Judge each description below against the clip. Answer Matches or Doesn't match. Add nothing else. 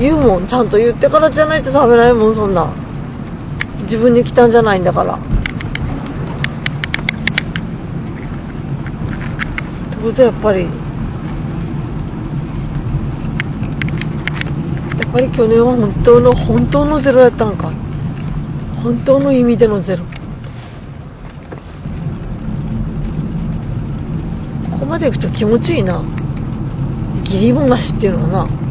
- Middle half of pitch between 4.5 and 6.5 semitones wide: Matches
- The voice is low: Doesn't match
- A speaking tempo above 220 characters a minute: Doesn't match